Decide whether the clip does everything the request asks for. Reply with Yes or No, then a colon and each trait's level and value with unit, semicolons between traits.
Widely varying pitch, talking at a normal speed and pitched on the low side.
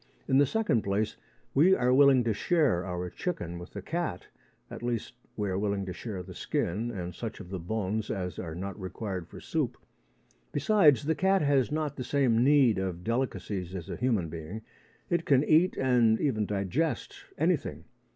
Yes: wide, 7.0 semitones; average, 180 wpm; low, 115 Hz